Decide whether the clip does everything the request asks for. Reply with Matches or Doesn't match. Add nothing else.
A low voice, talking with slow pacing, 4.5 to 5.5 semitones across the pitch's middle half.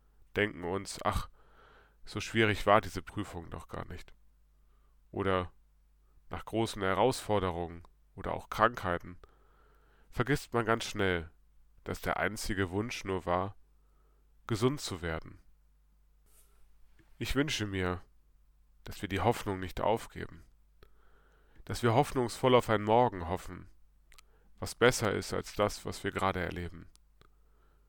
Matches